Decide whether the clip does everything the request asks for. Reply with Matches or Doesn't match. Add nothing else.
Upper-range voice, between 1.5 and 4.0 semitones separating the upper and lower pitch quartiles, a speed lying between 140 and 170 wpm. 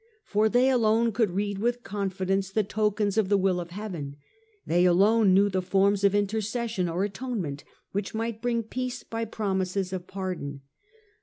Matches